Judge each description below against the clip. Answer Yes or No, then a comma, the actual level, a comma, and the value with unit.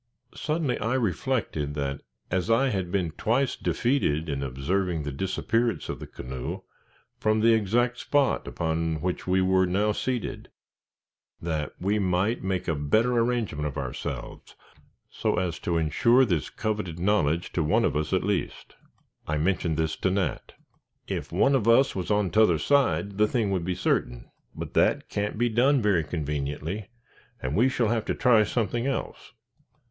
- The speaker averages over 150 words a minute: Yes, average, 165 wpm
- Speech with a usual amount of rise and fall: No, wide, 6.1 semitones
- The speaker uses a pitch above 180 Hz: No, very low, 95 Hz